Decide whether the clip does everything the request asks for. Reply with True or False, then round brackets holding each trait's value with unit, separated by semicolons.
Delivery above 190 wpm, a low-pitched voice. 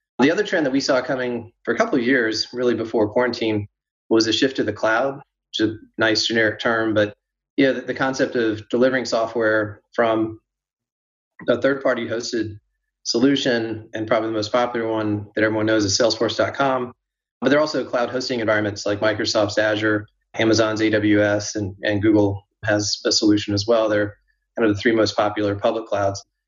False (180 wpm; 110 Hz)